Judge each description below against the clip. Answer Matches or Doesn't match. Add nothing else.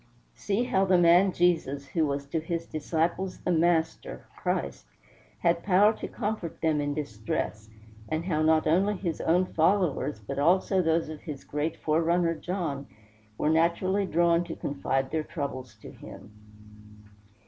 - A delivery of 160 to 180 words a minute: Doesn't match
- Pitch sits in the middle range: Matches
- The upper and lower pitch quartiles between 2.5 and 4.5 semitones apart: Matches